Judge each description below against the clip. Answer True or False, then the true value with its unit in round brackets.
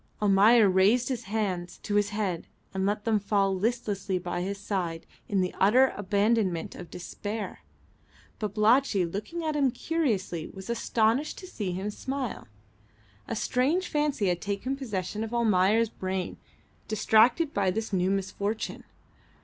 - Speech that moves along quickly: False (140 wpm)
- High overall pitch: True (210 Hz)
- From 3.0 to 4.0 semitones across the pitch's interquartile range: True (3.6 semitones)